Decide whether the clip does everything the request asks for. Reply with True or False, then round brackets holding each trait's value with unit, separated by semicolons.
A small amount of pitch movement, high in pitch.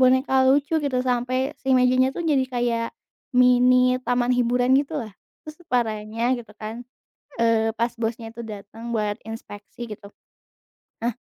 True (2.3 semitones; 245 Hz)